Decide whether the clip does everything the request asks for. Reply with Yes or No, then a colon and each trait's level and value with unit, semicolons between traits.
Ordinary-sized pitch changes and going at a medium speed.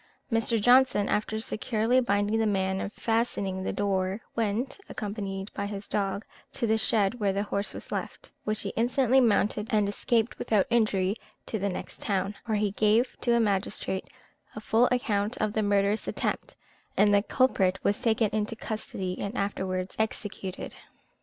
No: narrow, 2.1 semitones; average, 165 wpm